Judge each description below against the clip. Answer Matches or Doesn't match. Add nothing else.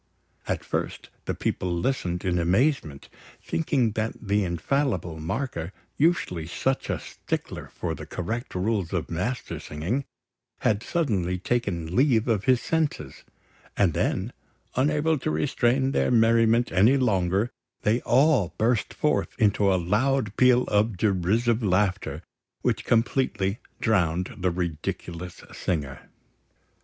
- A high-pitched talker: Doesn't match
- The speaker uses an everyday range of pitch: Doesn't match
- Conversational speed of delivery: Doesn't match